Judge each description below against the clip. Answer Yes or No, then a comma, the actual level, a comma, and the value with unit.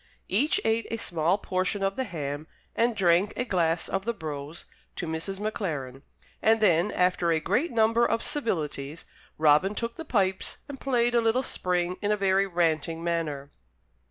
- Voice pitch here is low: No, high, 190 Hz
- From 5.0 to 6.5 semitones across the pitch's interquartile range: Yes, wide, 5.5 semitones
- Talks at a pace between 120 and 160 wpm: No, average, 170 wpm